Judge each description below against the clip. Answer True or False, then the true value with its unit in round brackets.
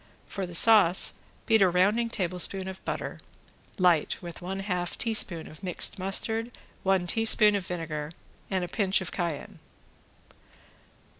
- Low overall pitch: False (185 Hz)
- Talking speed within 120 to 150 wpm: True (140 wpm)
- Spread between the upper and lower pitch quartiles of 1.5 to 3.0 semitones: True (2.6 semitones)